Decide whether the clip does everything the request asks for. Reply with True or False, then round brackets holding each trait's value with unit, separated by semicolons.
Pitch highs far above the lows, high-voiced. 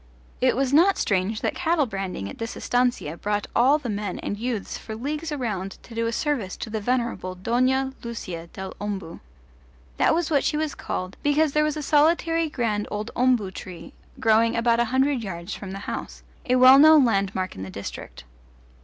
True (5.9 semitones; 235 Hz)